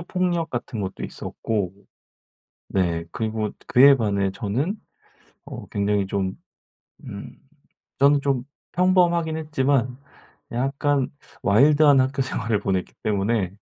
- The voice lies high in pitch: No, low, 125 Hz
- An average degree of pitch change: No, wide, 6.1 semitones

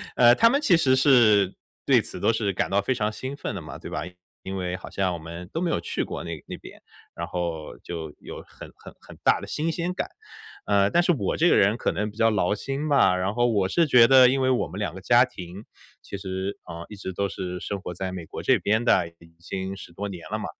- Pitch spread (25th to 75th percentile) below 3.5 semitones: No, wide, 5.6 semitones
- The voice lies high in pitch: No, low, 100 Hz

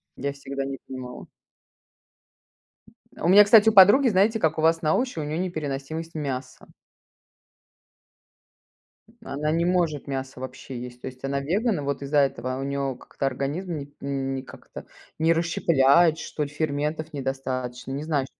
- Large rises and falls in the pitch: No, average, 3.5 semitones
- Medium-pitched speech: Yes, medium, 145 Hz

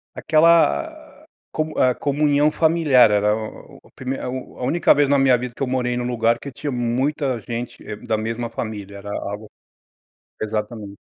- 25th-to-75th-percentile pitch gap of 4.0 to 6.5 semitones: Yes, average, 4.4 semitones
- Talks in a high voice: No, low, 125 Hz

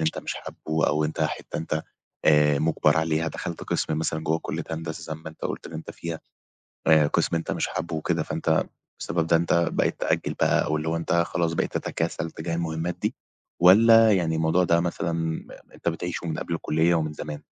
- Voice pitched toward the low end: Yes, very low, 80 Hz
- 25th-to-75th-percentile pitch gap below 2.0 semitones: Yes, narrow, 1.2 semitones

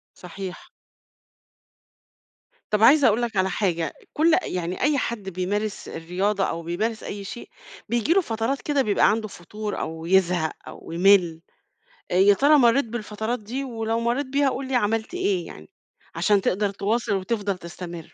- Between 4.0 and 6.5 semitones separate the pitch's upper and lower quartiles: Yes, average, 4.3 semitones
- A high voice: Yes, high, 210 Hz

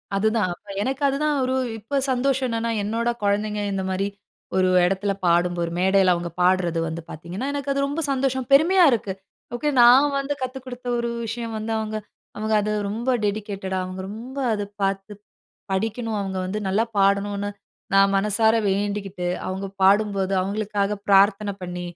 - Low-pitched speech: No, high, 205 Hz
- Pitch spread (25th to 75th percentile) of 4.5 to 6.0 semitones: No, average, 3.5 semitones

